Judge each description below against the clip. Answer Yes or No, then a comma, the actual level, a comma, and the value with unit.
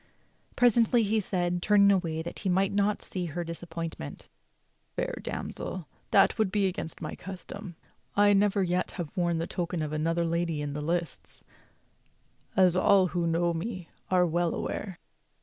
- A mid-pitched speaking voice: Yes, medium, 180 Hz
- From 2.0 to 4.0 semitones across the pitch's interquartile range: Yes, average, 2.8 semitones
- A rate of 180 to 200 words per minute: No, average, 160 wpm